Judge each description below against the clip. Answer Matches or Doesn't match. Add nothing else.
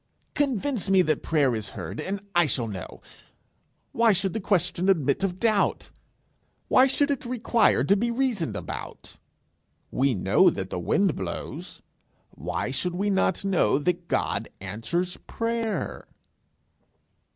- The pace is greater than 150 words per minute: Doesn't match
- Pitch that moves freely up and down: Matches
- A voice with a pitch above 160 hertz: Matches